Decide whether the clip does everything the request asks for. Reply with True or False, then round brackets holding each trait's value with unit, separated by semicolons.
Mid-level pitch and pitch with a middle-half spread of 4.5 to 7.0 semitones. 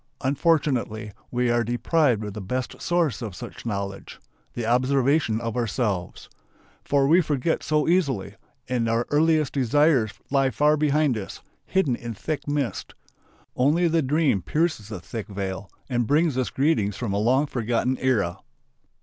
False (125 Hz; 5.1 semitones)